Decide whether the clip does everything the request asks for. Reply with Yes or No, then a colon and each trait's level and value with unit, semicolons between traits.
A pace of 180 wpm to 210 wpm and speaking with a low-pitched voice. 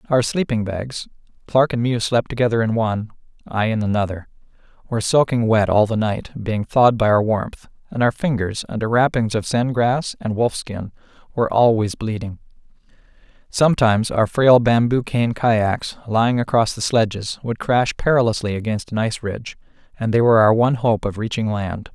No: average, 170 wpm; low, 115 Hz